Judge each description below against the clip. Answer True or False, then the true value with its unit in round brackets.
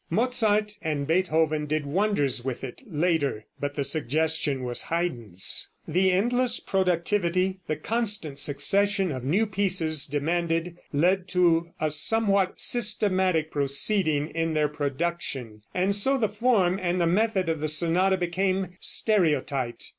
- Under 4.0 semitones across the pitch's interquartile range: False (4.6 semitones)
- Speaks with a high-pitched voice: False (170 Hz)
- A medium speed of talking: False (130 wpm)